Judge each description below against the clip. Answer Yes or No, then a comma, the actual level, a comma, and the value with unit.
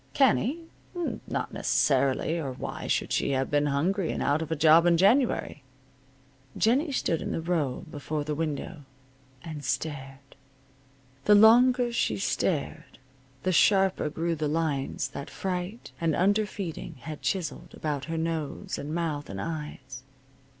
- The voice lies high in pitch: No, medium, 160 Hz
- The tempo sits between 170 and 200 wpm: No, average, 145 wpm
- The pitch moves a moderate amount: Yes, average, 4.5 semitones